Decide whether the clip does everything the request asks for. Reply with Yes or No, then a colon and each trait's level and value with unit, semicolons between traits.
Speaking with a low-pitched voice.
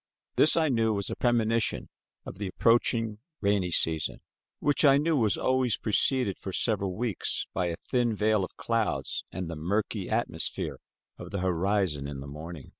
Yes: low, 105 Hz